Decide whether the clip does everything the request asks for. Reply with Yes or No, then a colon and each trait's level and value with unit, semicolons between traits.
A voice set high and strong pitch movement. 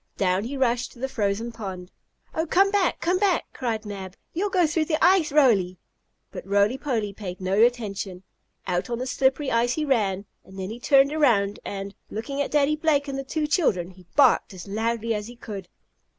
Yes: high, 235 Hz; wide, 6.4 semitones